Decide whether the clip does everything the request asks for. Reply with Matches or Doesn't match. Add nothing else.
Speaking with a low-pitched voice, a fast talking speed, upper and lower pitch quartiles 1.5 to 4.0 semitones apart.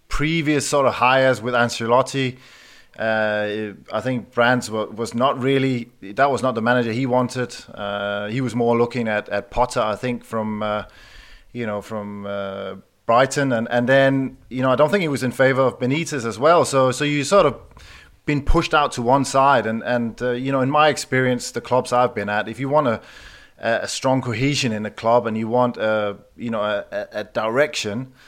Matches